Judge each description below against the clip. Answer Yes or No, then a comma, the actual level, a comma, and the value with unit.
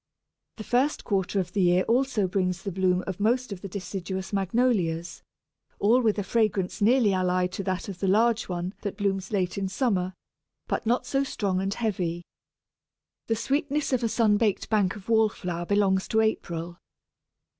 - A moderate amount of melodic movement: Yes, average, 3.4 semitones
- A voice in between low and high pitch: No, high, 195 Hz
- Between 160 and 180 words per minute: Yes, average, 175 wpm